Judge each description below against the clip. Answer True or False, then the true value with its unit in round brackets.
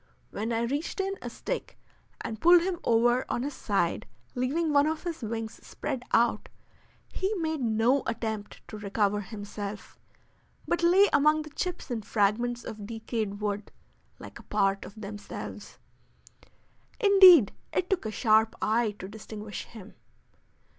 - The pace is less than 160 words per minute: True (145 wpm)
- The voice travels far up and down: True (6.5 semitones)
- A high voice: True (230 Hz)